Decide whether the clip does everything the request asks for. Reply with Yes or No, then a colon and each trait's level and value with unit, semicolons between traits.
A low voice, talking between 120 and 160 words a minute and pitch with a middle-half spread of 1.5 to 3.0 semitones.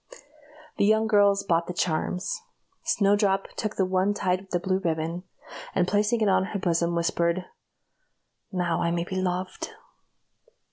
No: medium, 185 Hz; average, 145 wpm; average, 2.7 semitones